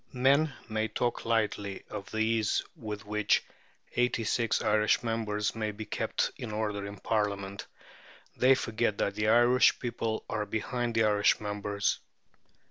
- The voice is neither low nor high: No, low, 110 Hz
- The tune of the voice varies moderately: No, narrow, 1.8 semitones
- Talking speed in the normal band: Yes, average, 145 wpm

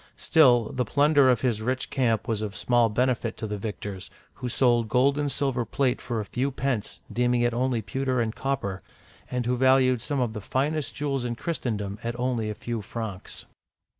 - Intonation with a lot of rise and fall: No, average, 2.9 semitones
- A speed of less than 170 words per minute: No, average, 200 wpm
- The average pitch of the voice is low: Yes, low, 120 Hz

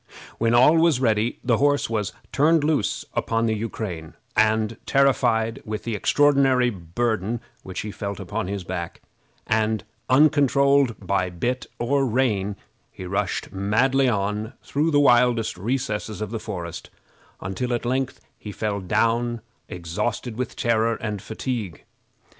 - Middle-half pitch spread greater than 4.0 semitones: No, average, 3.6 semitones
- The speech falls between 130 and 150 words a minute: Yes, average, 140 wpm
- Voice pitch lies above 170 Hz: No, low, 115 Hz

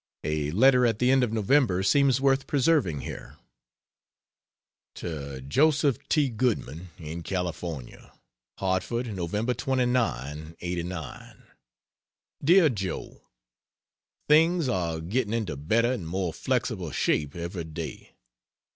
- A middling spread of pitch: No, wide, 7.7 semitones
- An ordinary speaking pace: No, slow, 110 wpm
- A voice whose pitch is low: Yes, low, 100 Hz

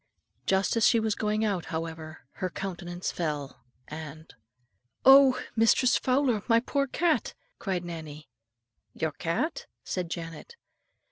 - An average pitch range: No, wide, 6.2 semitones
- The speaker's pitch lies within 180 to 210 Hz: Yes, medium, 185 Hz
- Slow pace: Yes, slow, 125 wpm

